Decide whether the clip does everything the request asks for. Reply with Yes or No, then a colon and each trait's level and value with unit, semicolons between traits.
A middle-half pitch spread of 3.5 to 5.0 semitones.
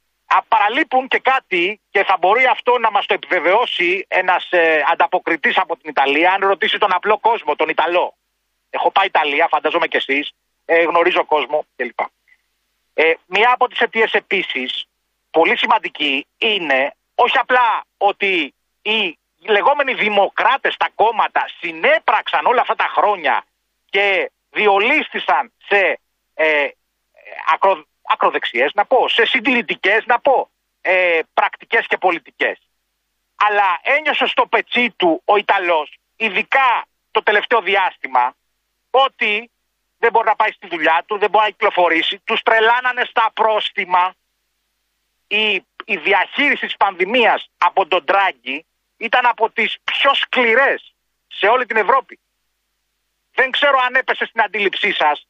No: wide, 5.6 semitones